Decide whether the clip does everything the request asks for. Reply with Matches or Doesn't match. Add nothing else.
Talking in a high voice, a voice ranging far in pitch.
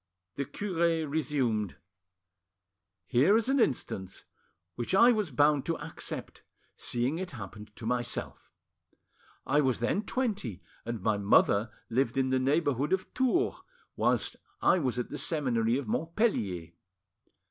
Doesn't match